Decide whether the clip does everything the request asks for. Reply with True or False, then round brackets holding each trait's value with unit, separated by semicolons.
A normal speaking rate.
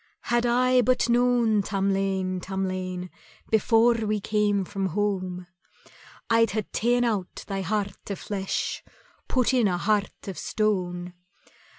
False (125 wpm)